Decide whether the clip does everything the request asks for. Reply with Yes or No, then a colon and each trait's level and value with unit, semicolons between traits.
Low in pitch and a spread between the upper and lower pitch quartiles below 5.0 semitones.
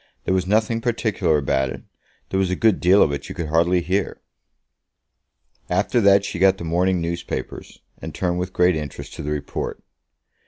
Yes: very low, 90 Hz; average, 2.8 semitones